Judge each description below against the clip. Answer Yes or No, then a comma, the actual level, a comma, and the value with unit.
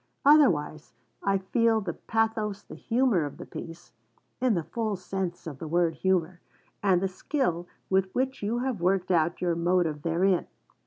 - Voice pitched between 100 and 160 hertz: No, medium, 185 Hz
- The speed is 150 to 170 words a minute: Yes, average, 165 wpm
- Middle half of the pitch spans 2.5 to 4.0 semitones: No, average, 4.5 semitones